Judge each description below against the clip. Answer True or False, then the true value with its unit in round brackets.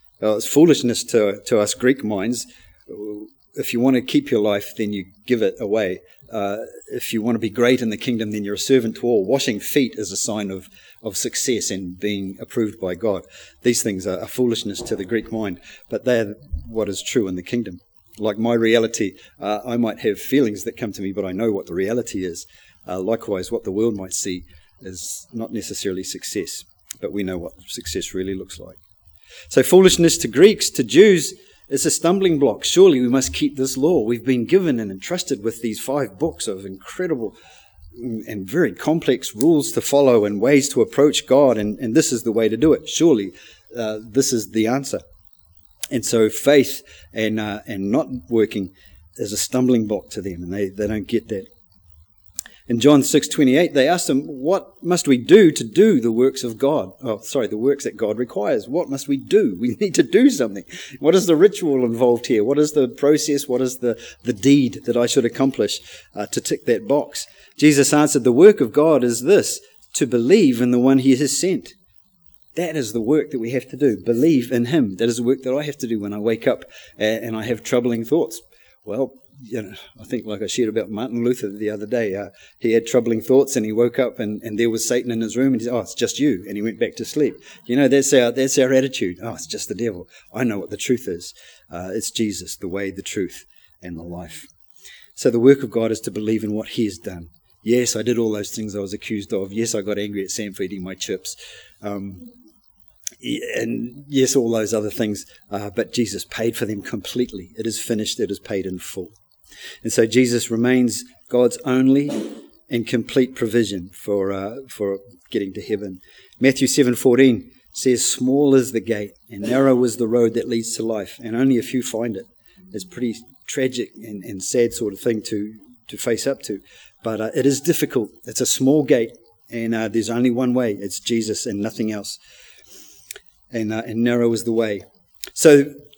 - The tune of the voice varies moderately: True (4.1 semitones)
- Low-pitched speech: True (115 Hz)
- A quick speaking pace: True (215 wpm)